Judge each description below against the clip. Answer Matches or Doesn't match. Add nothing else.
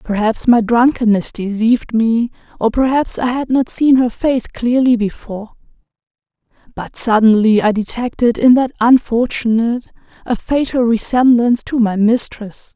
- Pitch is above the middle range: Matches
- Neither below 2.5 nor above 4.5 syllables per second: Doesn't match